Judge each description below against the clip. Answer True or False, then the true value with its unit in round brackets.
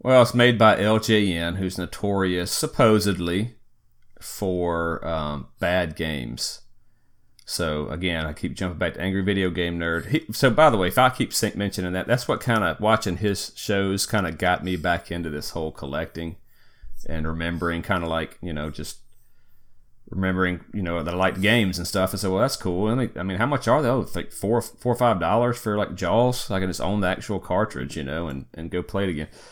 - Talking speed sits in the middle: False (215 wpm)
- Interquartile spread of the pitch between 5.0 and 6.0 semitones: False (4.3 semitones)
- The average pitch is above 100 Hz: False (95 Hz)